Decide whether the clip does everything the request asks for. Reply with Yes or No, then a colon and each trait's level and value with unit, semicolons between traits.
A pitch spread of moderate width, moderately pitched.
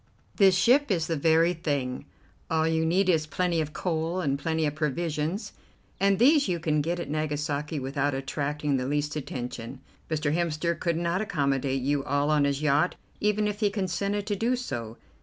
Yes: average, 4.0 semitones; medium, 160 Hz